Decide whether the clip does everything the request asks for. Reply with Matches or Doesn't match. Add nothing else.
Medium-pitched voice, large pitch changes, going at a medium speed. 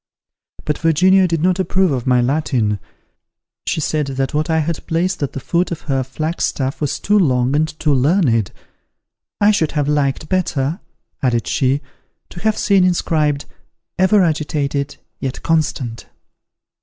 Doesn't match